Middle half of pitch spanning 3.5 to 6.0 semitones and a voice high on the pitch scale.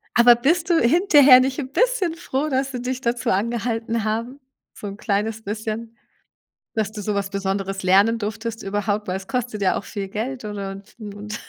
Yes: average, 3.8 semitones; high, 225 Hz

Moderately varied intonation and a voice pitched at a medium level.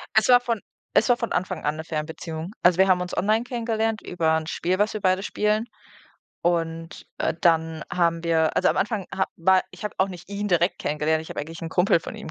Yes: average, 4.2 semitones; medium, 180 Hz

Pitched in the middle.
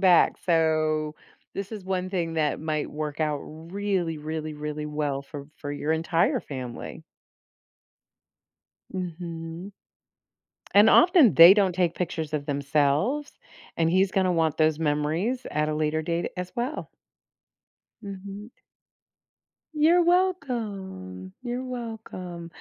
Yes: medium, 165 Hz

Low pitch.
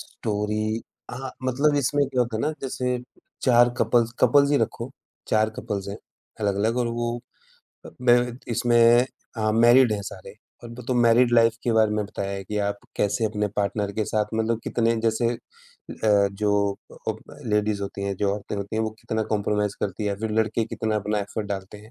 Yes: low, 110 Hz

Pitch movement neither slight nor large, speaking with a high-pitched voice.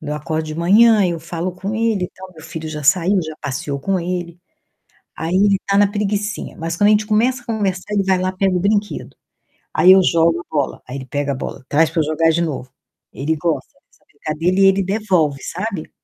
No: average, 4.0 semitones; medium, 180 Hz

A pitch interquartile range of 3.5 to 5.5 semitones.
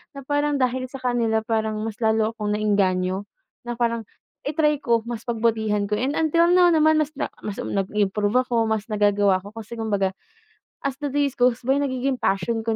Yes: average, 4.1 semitones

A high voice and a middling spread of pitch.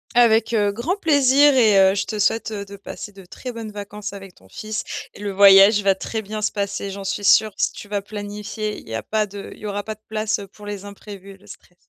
No: high, 205 Hz; narrow, 1.6 semitones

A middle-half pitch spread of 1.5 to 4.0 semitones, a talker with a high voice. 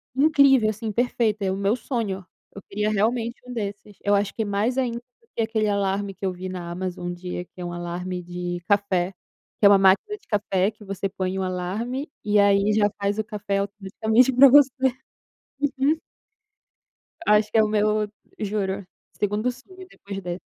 Yes: average, 2.9 semitones; high, 205 Hz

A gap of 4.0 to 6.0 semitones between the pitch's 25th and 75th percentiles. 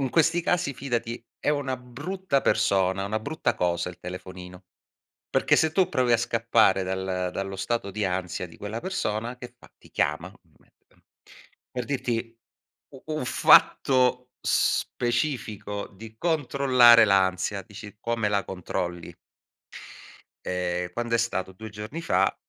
Yes: average, 5.1 semitones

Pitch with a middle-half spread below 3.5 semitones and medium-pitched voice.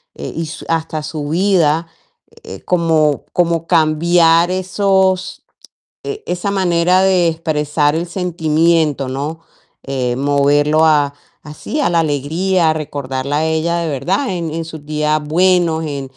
Yes: average, 2.8 semitones; medium, 160 Hz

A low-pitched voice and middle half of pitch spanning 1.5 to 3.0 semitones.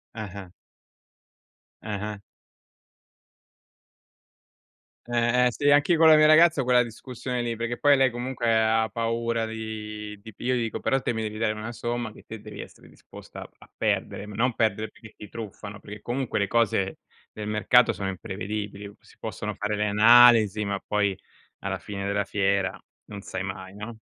Yes: low, 110 Hz; narrow, 2.6 semitones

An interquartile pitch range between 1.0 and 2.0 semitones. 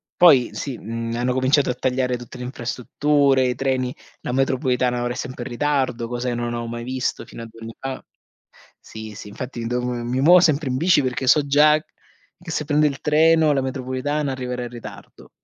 No: average, 2.7 semitones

